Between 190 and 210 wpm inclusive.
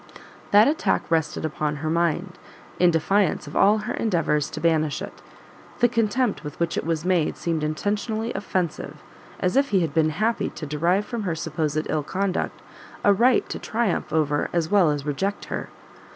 No: average, 180 wpm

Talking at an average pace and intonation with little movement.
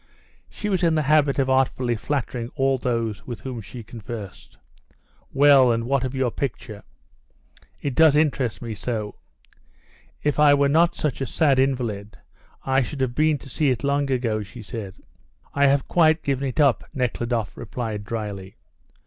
No: average, 165 wpm; average, 3.7 semitones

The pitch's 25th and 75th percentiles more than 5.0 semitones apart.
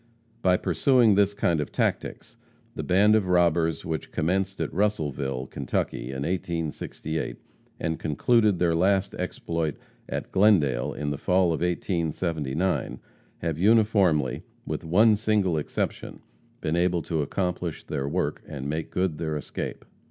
No: average, 3.7 semitones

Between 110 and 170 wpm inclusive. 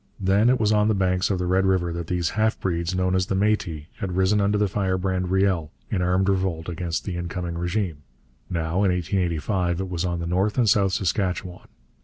No: fast, 205 wpm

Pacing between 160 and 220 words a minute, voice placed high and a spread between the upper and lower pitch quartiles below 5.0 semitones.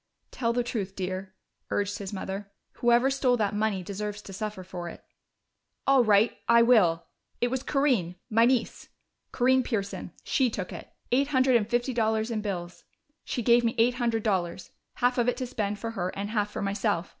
Yes: average, 190 wpm; high, 220 Hz; average, 3.5 semitones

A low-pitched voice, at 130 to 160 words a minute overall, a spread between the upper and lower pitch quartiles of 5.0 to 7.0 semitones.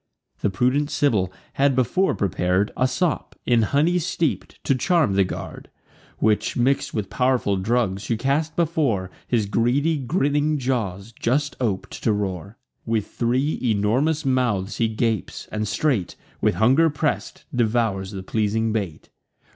Yes: low, 120 Hz; average, 140 wpm; wide, 5.5 semitones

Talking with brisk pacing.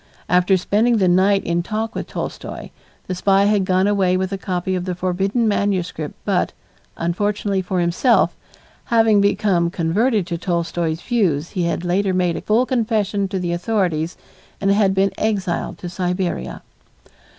No: average, 160 wpm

